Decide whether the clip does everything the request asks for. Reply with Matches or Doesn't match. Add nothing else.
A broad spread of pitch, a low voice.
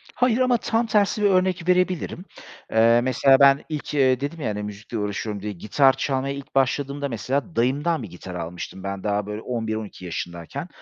Matches